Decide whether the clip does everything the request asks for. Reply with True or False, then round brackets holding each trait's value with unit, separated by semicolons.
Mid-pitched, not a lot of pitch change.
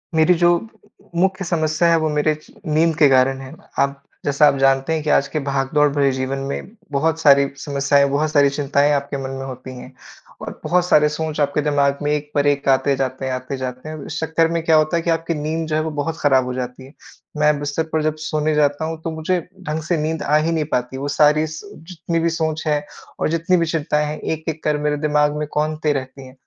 True (150 Hz; 2.3 semitones)